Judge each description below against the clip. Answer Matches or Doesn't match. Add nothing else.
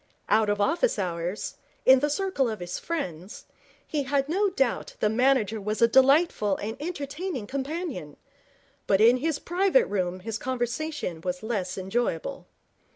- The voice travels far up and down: Matches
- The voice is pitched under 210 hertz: Doesn't match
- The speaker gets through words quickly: Doesn't match